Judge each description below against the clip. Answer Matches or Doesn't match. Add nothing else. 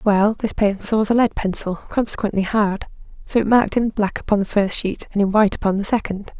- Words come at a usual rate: Doesn't match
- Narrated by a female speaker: Matches